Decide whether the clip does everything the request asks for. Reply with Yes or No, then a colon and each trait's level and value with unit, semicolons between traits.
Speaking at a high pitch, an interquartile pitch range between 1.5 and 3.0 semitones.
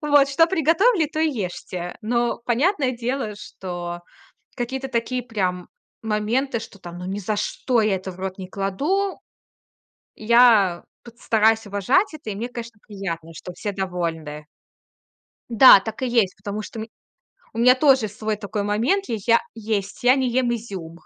No: high, 220 Hz; average, 4.5 semitones